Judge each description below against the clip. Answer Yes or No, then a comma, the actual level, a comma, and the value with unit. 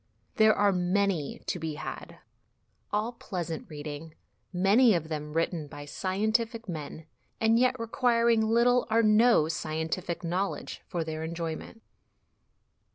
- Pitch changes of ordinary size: No, wide, 5.8 semitones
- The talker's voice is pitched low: No, medium, 185 Hz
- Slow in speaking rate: Yes, slow, 130 wpm